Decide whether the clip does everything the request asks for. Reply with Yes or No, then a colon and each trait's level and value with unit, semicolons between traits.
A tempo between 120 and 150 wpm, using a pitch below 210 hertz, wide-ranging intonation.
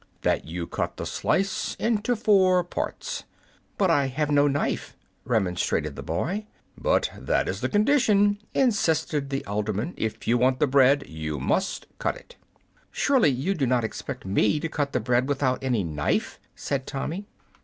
No: average, 165 wpm; medium, 140 Hz; wide, 8.0 semitones